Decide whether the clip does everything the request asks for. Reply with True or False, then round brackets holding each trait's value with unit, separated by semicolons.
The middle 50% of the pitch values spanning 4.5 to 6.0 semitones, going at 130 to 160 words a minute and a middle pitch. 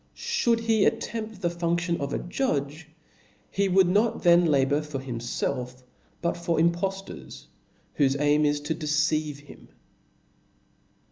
False (4.0 semitones; 135 wpm; 160 Hz)